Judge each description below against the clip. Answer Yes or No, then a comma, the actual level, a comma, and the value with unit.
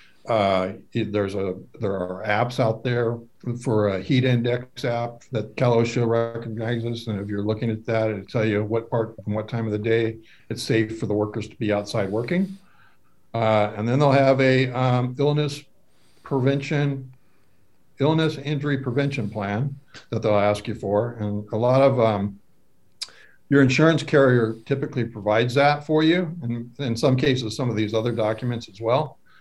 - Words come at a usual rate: Yes, average, 175 wpm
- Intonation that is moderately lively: Yes, average, 3.9 semitones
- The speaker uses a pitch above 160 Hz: No, low, 115 Hz